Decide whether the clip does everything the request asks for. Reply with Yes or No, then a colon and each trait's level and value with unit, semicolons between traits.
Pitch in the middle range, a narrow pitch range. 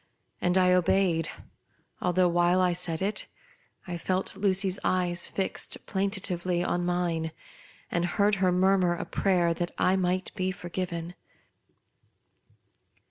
Yes: medium, 180 Hz; narrow, 1.4 semitones